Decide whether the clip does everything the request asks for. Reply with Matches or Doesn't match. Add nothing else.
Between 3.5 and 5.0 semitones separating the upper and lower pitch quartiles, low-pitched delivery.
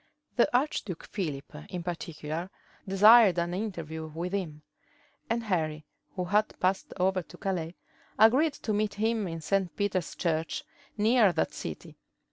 Doesn't match